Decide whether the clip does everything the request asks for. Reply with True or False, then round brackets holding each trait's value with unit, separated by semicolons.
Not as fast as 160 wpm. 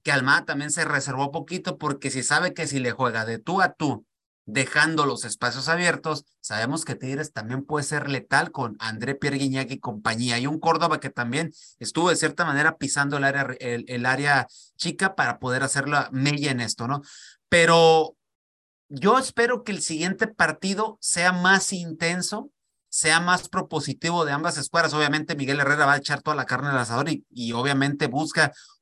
False (185 wpm)